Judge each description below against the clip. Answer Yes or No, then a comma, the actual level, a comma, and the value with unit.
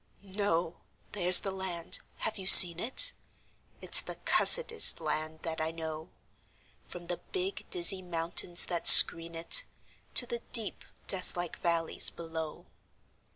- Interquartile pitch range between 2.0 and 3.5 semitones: Yes, average, 2.9 semitones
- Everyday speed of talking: No, slow, 130 wpm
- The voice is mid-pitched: Yes, medium, 175 Hz